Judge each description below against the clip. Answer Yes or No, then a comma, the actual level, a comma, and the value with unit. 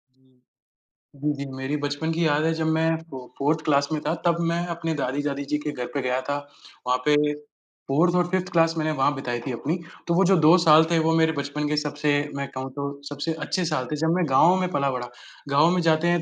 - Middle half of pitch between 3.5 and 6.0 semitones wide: No, average, 2.7 semitones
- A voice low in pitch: No, medium, 150 Hz